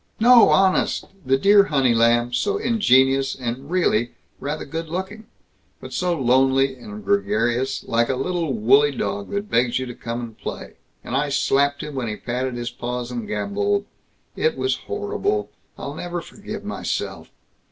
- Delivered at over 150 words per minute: Yes, average, 165 wpm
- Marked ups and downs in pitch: Yes, wide, 7.6 semitones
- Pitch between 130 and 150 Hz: Yes, low, 135 Hz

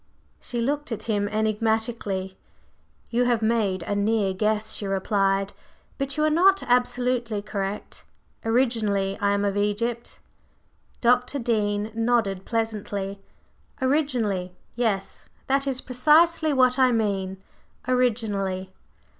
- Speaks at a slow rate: Yes, slow, 115 wpm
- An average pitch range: Yes, average, 3.6 semitones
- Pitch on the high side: Yes, high, 225 Hz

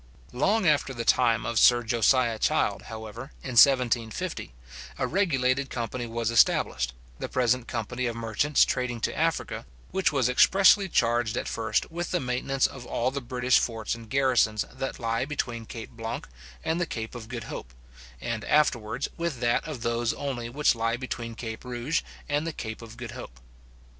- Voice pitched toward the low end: Yes, low, 120 Hz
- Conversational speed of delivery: Yes, average, 175 wpm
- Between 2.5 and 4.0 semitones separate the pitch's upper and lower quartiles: Yes, average, 3.0 semitones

